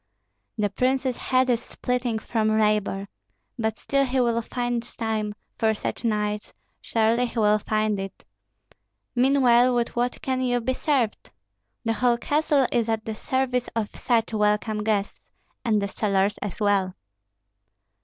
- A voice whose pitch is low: No, high, 225 Hz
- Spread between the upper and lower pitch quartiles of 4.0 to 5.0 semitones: No, average, 2.8 semitones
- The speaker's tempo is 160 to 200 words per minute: No, average, 145 wpm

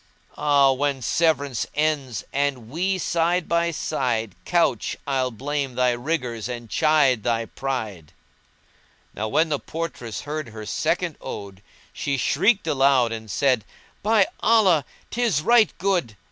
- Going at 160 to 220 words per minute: No, slow, 135 wpm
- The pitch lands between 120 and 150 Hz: Yes, medium, 140 Hz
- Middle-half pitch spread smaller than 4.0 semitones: No, average, 5.3 semitones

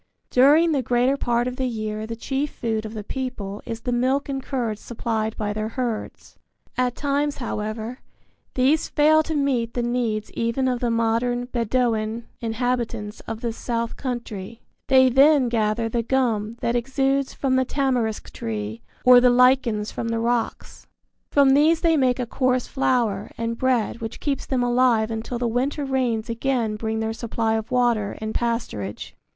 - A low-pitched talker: No, high, 240 Hz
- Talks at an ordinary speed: Yes, average, 170 wpm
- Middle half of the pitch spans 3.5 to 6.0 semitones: No, average, 2.7 semitones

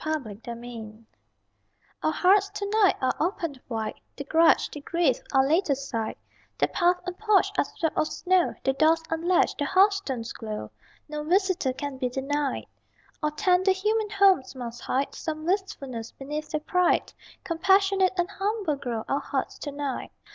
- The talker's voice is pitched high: Yes, very high, 310 Hz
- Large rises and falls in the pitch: Yes, wide, 5.9 semitones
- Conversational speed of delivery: Yes, average, 160 wpm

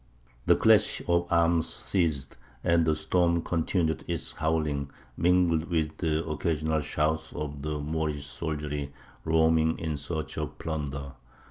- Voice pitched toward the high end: No, very low, 80 Hz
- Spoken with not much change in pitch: Yes, narrow, 1.7 semitones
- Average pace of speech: No, slow, 130 wpm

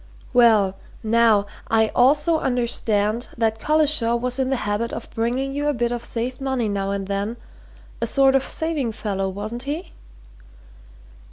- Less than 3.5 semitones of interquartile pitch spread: No, average, 3.8 semitones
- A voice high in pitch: Yes, high, 235 Hz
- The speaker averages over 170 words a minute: No, average, 155 wpm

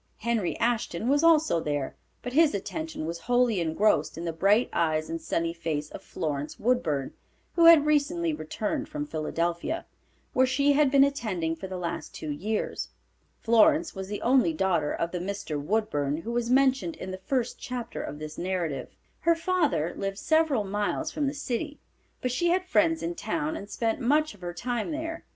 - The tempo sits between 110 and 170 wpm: No, average, 180 wpm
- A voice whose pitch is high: Yes, high, 225 Hz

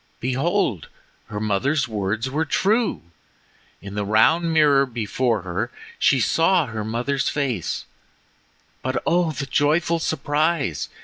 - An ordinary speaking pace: No, slow, 120 wpm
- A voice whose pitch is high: No, low, 135 Hz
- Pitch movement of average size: No, wide, 6.6 semitones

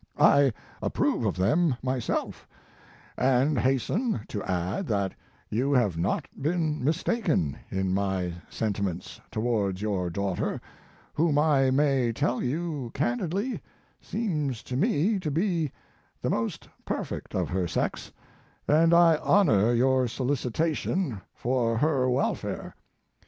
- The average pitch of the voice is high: No, low, 130 Hz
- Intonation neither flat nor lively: No, wide, 6.7 semitones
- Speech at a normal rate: No, slow, 120 wpm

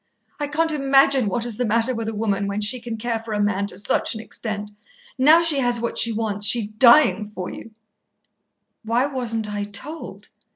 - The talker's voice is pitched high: Yes, high, 230 Hz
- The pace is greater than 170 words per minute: Yes, average, 200 wpm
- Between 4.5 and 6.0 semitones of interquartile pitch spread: No, average, 3.6 semitones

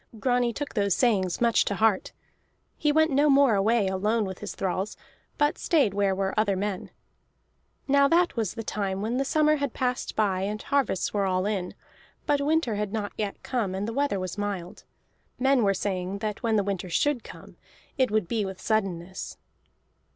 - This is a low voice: No, high, 210 Hz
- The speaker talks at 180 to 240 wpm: Yes, average, 185 wpm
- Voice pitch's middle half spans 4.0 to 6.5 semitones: Yes, average, 4.8 semitones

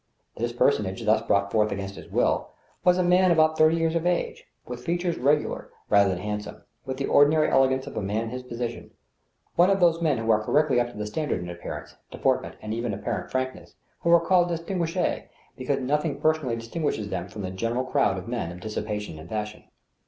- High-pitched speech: No, low, 125 Hz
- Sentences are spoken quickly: Yes, fast, 215 wpm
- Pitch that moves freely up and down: Yes, wide, 7.0 semitones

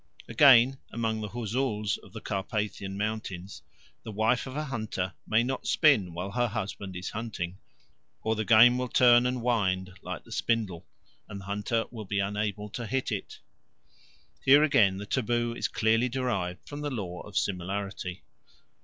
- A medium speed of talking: Yes, average, 165 wpm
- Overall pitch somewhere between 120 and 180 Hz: No, low, 110 Hz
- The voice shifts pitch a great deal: No, average, 3.7 semitones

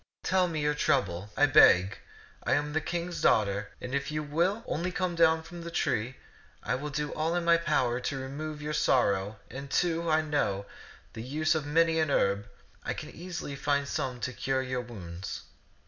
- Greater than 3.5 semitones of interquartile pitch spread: Yes, average, 4.5 semitones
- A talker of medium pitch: Yes, medium, 145 Hz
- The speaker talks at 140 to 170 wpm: No, average, 195 wpm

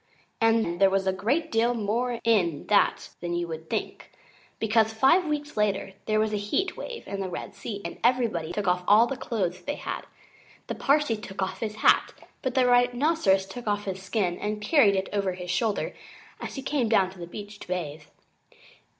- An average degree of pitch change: Yes, average, 4.1 semitones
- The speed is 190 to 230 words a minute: Yes, average, 200 wpm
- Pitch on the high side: Yes, high, 210 Hz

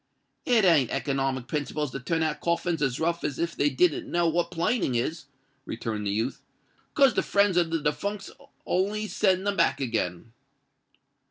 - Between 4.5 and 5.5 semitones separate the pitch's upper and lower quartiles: Yes, average, 5.1 semitones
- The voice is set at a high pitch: No, medium, 165 Hz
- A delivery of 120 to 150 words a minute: No, average, 170 wpm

